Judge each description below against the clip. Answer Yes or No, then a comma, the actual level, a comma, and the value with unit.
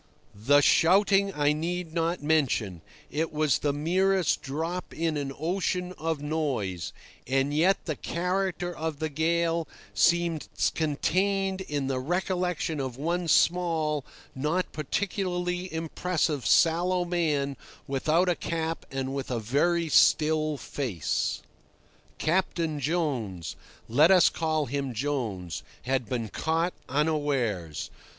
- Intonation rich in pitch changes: No, average, 4.0 semitones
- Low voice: No, medium, 155 Hz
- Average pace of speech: No, slow, 110 wpm